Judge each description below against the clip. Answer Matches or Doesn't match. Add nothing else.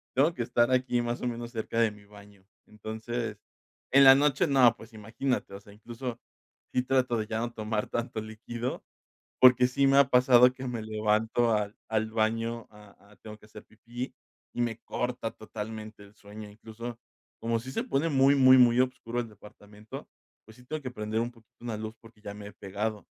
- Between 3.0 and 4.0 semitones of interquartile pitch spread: Doesn't match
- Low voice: Matches